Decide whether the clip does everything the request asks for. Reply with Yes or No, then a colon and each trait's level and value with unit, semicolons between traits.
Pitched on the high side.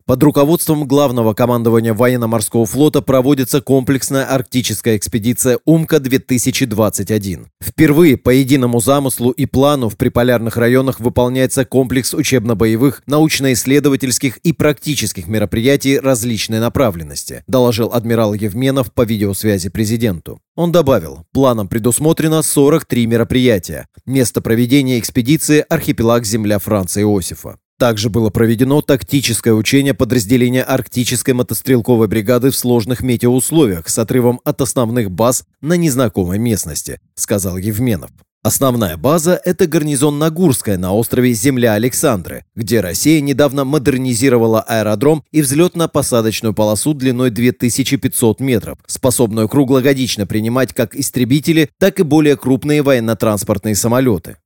No: low, 125 Hz